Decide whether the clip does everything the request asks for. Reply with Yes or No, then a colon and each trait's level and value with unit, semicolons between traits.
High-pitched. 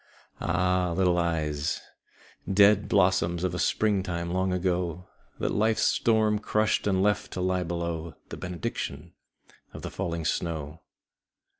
No: very low, 90 Hz